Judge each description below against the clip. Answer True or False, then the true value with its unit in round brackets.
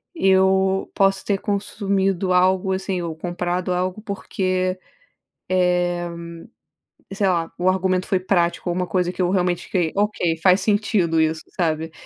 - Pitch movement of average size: False (1.6 semitones)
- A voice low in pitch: False (185 Hz)